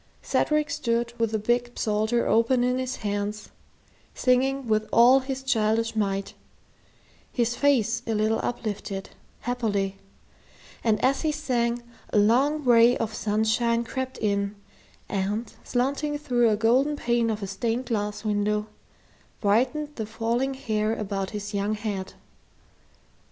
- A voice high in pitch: Yes, high, 230 Hz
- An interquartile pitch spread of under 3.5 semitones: Yes, average, 3.0 semitones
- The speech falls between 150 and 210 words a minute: No, slow, 135 wpm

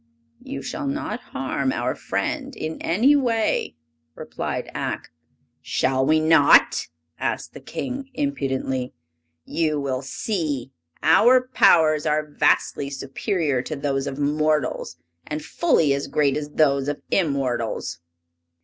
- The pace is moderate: No, slow, 120 wpm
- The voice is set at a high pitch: No, medium, 150 Hz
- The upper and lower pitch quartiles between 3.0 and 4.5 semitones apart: No, average, 4.9 semitones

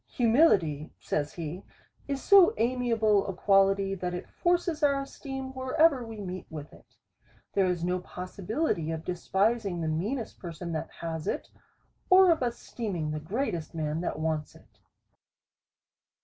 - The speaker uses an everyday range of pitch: No, wide, 7.4 semitones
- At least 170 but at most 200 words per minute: No, average, 145 wpm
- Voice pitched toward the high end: Yes, high, 195 Hz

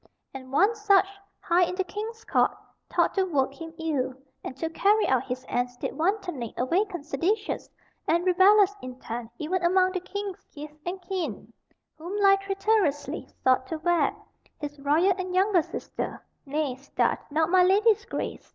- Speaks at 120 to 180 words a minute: Yes, average, 160 wpm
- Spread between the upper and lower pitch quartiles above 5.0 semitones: Yes, wide, 5.4 semitones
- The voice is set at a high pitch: Yes, very high, 345 Hz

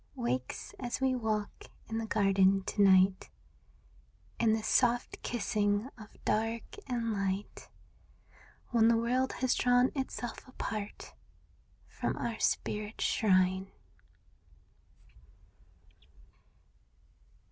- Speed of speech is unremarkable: No, slow, 95 wpm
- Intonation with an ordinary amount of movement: Yes, average, 3.4 semitones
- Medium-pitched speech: No, high, 220 Hz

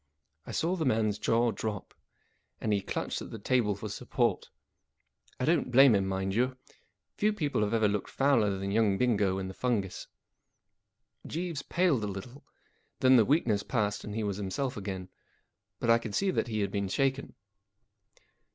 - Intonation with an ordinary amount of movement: Yes, average, 4.5 semitones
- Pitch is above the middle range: No, low, 110 Hz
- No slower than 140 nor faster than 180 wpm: Yes, average, 175 wpm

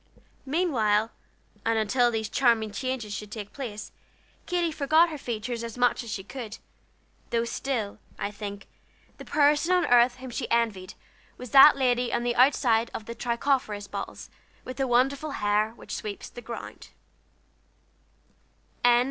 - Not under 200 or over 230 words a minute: No, average, 150 wpm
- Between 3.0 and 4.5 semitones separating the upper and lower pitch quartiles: Yes, average, 3.8 semitones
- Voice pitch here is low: No, high, 240 Hz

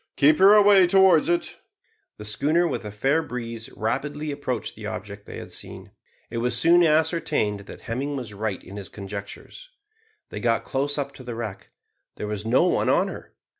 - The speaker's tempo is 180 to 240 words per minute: Yes, average, 185 wpm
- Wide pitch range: Yes, wide, 6.7 semitones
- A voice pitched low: Yes, low, 125 Hz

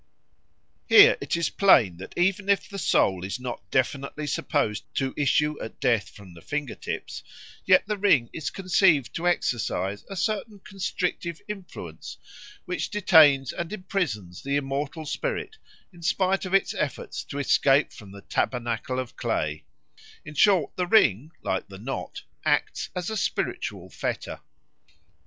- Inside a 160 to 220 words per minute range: No, average, 150 wpm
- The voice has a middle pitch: Yes, medium, 150 Hz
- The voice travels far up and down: Yes, wide, 7.4 semitones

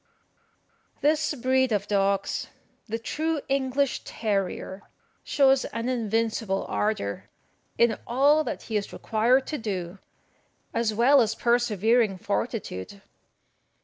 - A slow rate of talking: Yes, slow, 110 wpm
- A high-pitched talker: Yes, high, 230 Hz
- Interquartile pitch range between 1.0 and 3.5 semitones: No, average, 4.2 semitones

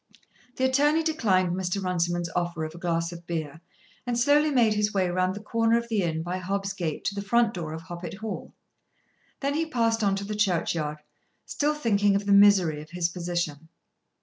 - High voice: Yes, high, 195 Hz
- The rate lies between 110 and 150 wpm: No, average, 200 wpm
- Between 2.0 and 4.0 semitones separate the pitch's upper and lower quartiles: No, average, 4.7 semitones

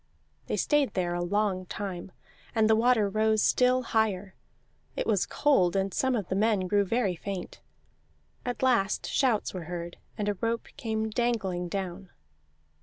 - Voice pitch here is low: No, high, 205 Hz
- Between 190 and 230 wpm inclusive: No, average, 160 wpm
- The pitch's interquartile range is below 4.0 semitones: Yes, average, 3.5 semitones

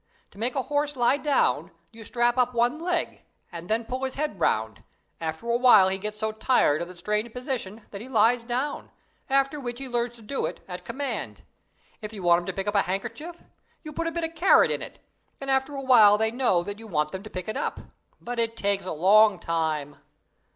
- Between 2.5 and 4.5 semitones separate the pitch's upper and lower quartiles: No, average, 5.2 semitones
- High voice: Yes, high, 230 Hz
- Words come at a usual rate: No, fast, 230 wpm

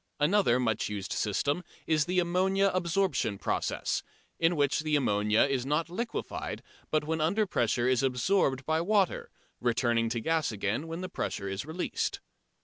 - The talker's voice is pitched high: No, medium, 150 Hz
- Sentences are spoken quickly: No, average, 155 wpm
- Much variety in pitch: Yes, wide, 6.8 semitones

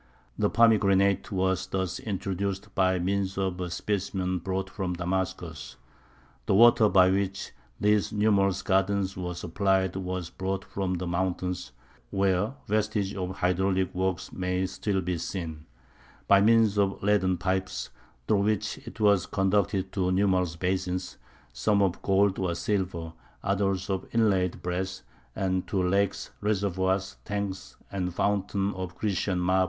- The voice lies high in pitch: No, very low, 95 Hz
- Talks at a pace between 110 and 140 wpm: Yes, slow, 135 wpm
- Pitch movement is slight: Yes, narrow, 1.4 semitones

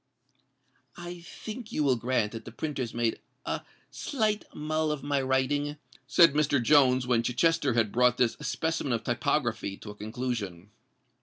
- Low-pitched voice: Yes, low, 130 Hz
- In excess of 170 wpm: No, average, 155 wpm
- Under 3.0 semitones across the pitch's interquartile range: No, average, 4.4 semitones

